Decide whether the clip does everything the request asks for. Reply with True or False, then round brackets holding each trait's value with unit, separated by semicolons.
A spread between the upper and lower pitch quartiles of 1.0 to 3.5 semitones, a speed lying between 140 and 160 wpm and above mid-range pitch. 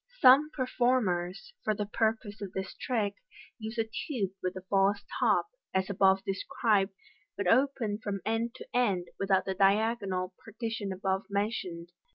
True (3.0 semitones; 150 wpm; 205 Hz)